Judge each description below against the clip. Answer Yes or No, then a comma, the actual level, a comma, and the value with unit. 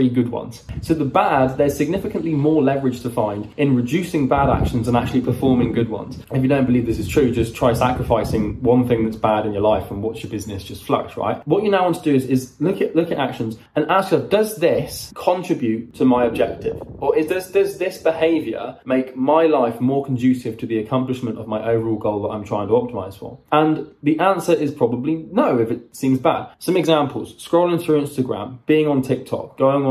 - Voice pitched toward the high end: No, low, 130 Hz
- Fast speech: Yes, fast, 220 wpm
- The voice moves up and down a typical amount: Yes, average, 4.9 semitones